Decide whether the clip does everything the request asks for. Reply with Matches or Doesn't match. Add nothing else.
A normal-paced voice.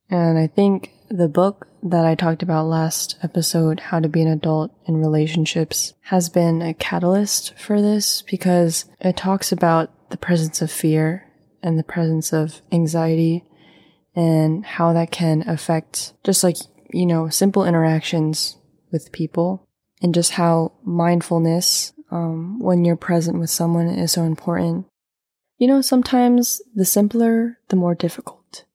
Matches